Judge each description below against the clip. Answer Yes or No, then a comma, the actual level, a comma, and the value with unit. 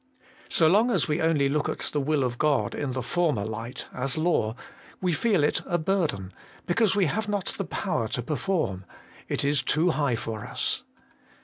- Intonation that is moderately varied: No, wide, 5.9 semitones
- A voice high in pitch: No, medium, 150 Hz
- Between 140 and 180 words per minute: No, average, 190 wpm